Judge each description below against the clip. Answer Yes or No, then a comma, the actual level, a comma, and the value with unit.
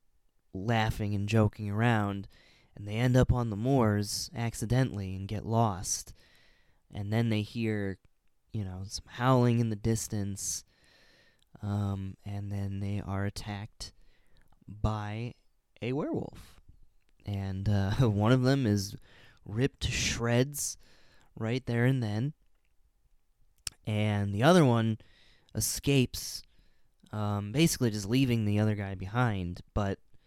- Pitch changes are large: No, average, 3.0 semitones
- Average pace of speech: No, slow, 125 wpm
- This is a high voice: No, low, 105 Hz